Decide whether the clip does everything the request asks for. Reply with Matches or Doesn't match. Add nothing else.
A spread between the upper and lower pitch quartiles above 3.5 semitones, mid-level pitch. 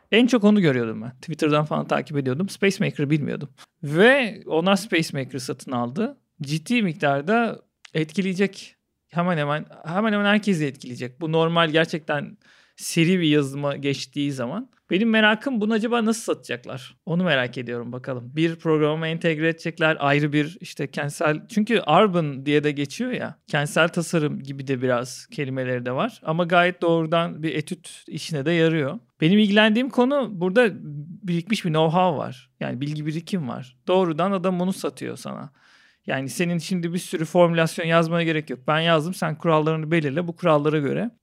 Matches